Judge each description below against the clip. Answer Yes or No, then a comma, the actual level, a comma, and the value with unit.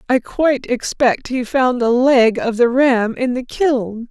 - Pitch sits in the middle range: No, very high, 250 Hz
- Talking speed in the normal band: Yes, average, 190 wpm